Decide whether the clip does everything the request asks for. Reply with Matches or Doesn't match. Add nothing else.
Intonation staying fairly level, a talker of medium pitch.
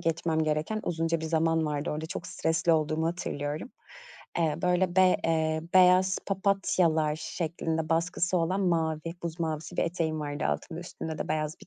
Matches